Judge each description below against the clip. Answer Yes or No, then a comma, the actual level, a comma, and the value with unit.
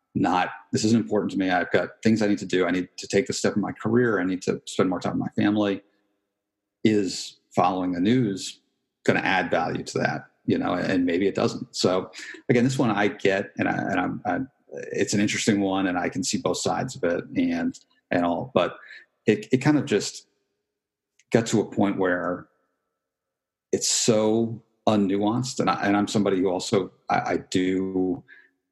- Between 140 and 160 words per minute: No, fast, 205 wpm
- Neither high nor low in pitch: No, low, 100 Hz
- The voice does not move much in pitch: No, average, 3.3 semitones